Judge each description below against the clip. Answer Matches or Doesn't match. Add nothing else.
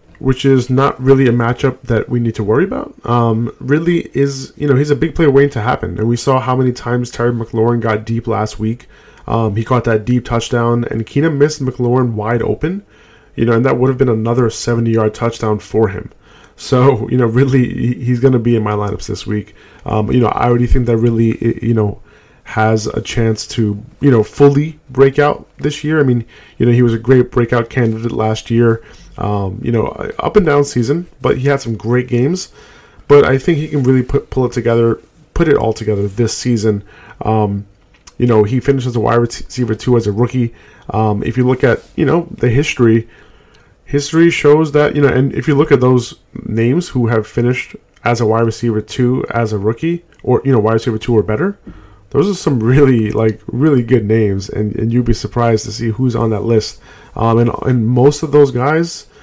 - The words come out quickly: Matches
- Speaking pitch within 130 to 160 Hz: Doesn't match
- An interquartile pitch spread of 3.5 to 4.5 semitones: Doesn't match